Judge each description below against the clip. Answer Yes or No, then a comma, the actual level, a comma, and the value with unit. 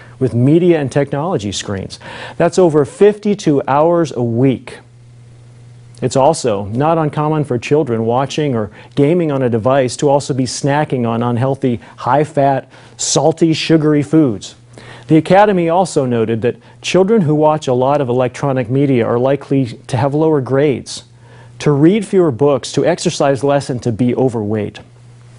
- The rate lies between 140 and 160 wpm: Yes, average, 150 wpm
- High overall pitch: No, low, 135 Hz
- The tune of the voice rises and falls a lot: No, average, 4.1 semitones